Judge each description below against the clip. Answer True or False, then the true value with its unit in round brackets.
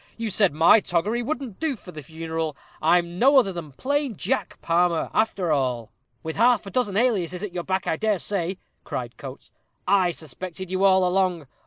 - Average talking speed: True (185 wpm)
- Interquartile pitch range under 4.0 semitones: False (4.4 semitones)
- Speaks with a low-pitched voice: False (185 Hz)